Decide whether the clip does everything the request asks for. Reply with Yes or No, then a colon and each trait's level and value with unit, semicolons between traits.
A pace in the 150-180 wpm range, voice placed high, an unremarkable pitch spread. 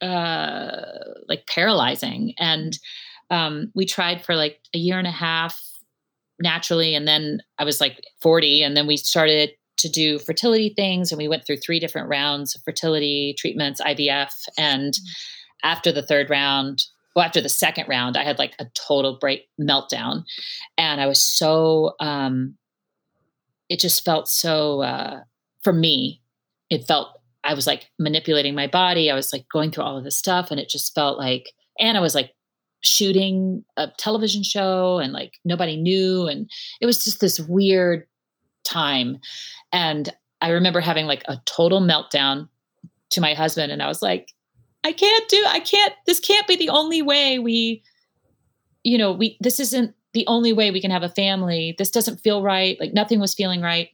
No: average, 175 wpm; medium, 165 Hz; average, 5.0 semitones